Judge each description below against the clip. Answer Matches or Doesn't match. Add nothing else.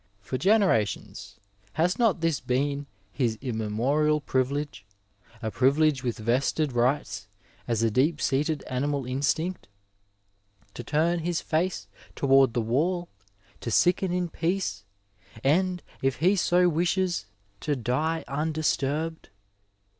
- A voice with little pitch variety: Doesn't match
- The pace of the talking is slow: Matches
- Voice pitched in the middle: Matches